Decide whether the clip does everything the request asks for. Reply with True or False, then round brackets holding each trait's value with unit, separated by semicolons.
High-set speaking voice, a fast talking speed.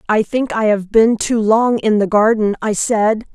True (215 Hz; 215 wpm)